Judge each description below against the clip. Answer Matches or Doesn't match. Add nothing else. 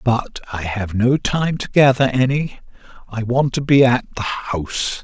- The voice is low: Matches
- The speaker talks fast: Doesn't match